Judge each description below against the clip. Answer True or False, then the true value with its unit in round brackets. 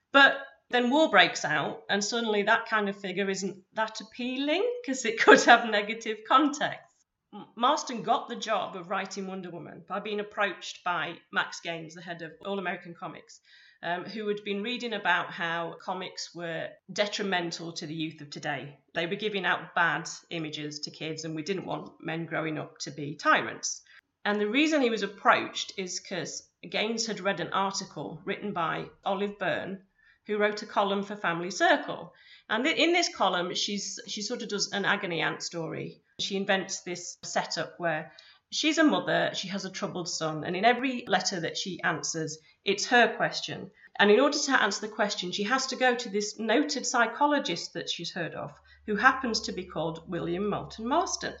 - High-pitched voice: True (200 Hz)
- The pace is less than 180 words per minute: False (185 wpm)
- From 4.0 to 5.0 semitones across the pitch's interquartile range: True (4.6 semitones)